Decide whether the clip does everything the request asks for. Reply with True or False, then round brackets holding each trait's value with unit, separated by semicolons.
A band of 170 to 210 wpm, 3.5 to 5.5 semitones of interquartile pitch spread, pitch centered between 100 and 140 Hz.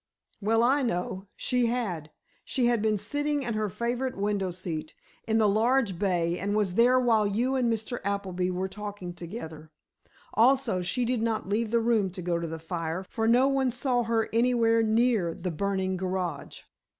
False (180 wpm; 4.5 semitones; 215 Hz)